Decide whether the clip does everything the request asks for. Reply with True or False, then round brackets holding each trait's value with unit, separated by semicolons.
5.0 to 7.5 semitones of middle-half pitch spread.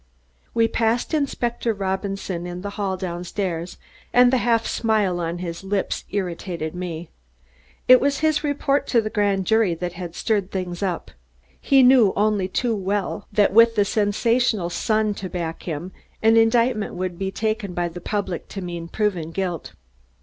False (4.1 semitones)